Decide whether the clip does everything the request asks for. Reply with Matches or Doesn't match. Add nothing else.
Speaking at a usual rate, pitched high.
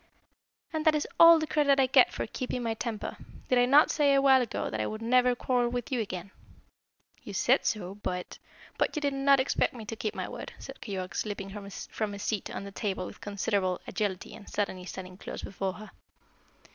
Doesn't match